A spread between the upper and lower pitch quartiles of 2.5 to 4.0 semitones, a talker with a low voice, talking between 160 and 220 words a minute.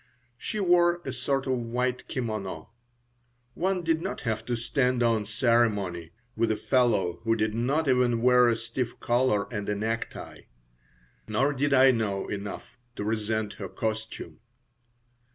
No: average, 3.0 semitones; low, 115 Hz; average, 150 wpm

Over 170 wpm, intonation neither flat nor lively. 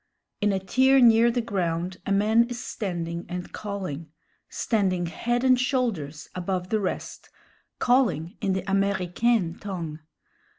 No: slow, 135 wpm; average, 4.9 semitones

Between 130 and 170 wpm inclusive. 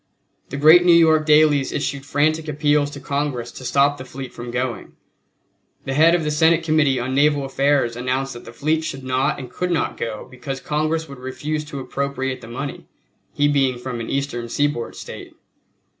No: average, 190 wpm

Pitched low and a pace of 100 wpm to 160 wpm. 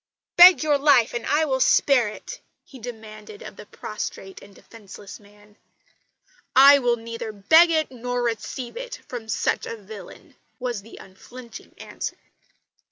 No: high, 235 Hz; average, 150 wpm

